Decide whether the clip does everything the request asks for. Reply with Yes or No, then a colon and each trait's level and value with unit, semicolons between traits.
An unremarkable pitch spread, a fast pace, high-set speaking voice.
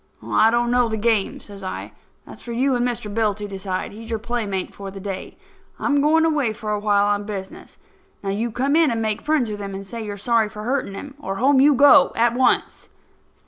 Yes: average, 3.5 semitones; fast, 230 wpm; high, 225 Hz